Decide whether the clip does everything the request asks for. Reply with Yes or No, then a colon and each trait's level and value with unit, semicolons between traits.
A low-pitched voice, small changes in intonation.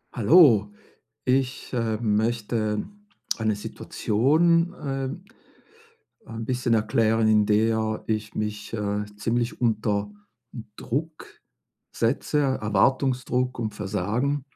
No: low, 115 Hz; average, 3.3 semitones